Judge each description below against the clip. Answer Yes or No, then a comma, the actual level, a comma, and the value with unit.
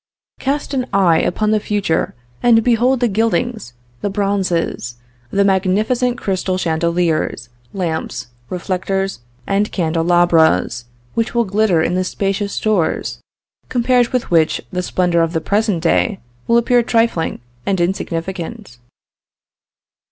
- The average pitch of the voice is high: Yes, high, 195 Hz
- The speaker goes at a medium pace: No, slow, 120 wpm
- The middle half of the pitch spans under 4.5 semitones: No, average, 4.8 semitones